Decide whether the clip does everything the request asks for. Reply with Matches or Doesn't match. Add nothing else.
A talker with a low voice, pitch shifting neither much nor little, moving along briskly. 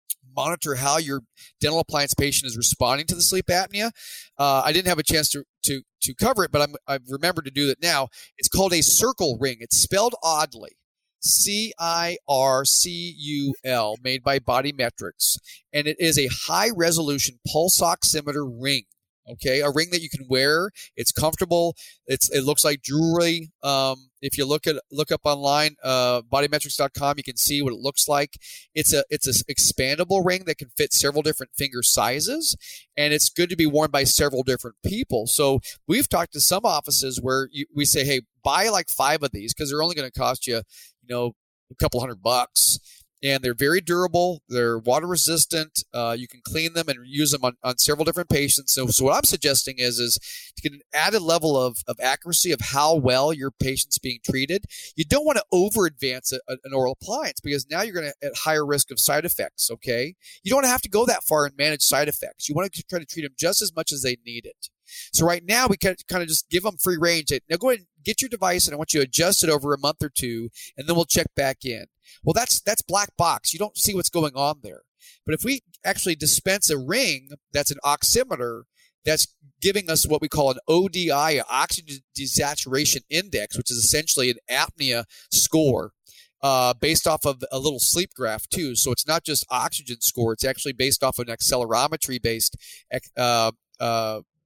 Doesn't match